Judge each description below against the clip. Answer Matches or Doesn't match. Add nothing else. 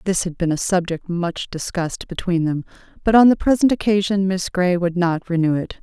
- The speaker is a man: Doesn't match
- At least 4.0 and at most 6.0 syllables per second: Matches